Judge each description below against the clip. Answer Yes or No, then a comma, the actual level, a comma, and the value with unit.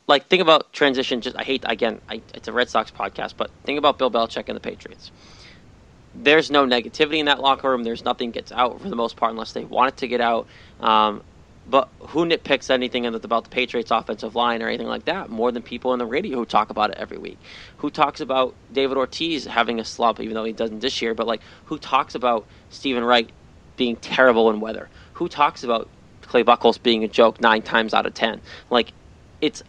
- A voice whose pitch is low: Yes, low, 125 Hz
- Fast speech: Yes, fast, 220 wpm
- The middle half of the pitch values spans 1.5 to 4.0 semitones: Yes, average, 3.2 semitones